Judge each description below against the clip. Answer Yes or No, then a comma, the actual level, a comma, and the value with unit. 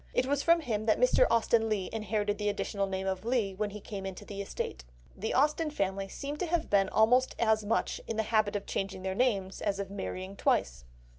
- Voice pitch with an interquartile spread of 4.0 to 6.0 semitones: No, average, 3.2 semitones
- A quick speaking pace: Yes, fast, 220 wpm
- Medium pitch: No, high, 210 Hz